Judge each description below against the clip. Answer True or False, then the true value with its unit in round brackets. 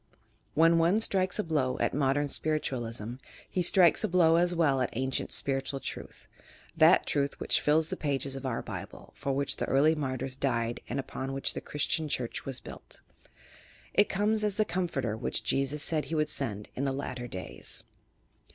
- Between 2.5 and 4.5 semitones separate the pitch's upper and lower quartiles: True (3.8 semitones)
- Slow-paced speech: False (190 wpm)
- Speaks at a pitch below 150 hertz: True (140 Hz)